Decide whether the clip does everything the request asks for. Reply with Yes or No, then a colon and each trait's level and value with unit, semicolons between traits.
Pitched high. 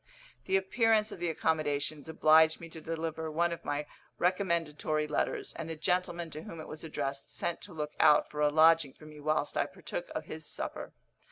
No: medium, 160 Hz